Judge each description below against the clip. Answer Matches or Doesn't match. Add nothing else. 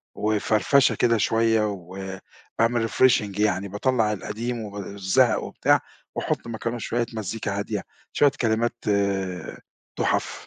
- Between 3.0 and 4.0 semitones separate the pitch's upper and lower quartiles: Doesn't match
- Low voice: Matches